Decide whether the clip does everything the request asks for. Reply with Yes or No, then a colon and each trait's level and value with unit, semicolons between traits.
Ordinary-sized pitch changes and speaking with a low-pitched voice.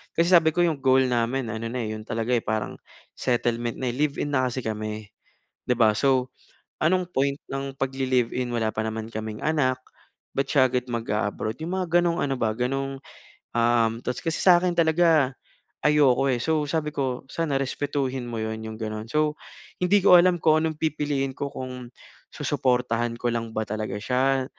Yes: average, 4.4 semitones; low, 130 Hz